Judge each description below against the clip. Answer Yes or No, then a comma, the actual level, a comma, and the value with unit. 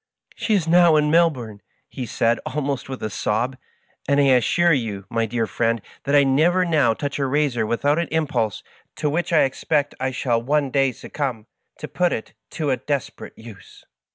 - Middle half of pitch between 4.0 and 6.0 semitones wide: Yes, average, 4.4 semitones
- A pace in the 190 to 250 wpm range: Yes, average, 195 wpm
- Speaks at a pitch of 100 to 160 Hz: Yes, low, 135 Hz